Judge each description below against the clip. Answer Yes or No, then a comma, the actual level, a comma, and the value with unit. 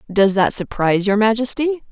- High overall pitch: Yes, high, 220 Hz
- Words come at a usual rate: Yes, average, 155 wpm